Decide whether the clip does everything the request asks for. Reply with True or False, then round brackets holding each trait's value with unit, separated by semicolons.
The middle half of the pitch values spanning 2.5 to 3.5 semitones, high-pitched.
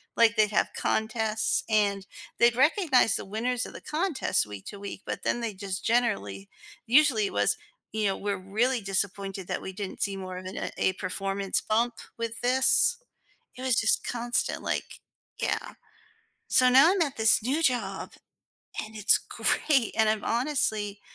False (4.0 semitones; 220 Hz)